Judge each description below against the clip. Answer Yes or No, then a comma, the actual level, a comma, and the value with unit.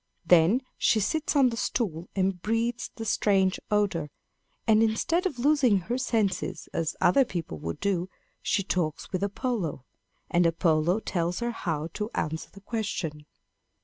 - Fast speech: No, average, 150 wpm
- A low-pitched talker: No, high, 200 Hz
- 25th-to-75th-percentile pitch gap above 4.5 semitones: Yes, wide, 5.4 semitones